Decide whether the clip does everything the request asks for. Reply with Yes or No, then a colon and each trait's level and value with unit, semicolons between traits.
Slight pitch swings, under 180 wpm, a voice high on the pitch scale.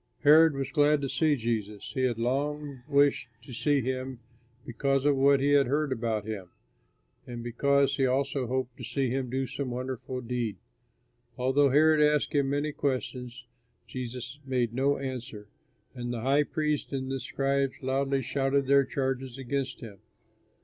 No: narrow, 2.1 semitones; average, 165 wpm; low, 135 Hz